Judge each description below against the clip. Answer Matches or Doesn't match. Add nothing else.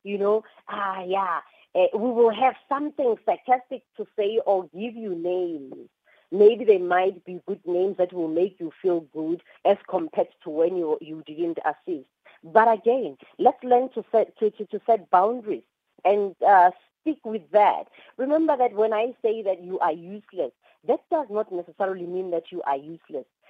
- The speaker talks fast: Doesn't match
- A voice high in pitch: Matches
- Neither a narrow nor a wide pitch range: Matches